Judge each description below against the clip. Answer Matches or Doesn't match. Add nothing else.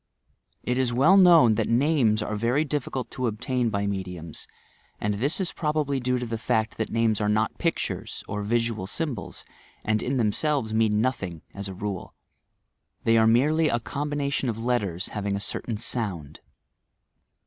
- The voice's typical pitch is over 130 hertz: Doesn't match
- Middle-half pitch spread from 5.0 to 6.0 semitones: Doesn't match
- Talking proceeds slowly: Doesn't match